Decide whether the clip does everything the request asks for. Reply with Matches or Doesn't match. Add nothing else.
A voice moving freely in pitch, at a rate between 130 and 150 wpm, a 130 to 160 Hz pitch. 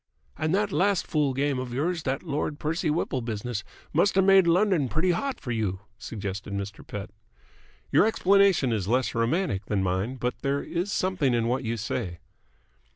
Doesn't match